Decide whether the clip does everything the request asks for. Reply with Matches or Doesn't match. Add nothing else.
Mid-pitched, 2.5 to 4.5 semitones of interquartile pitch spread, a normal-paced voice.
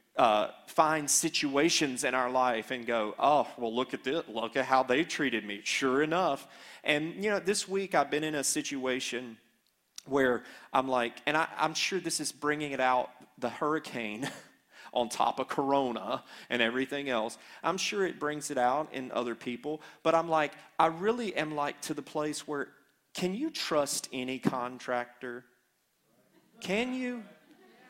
Matches